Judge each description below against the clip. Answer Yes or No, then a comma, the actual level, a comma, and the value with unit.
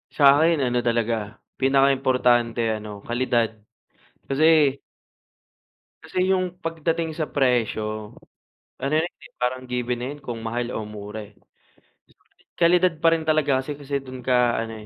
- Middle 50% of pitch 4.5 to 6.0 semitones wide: Yes, average, 4.8 semitones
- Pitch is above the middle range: No, low, 130 Hz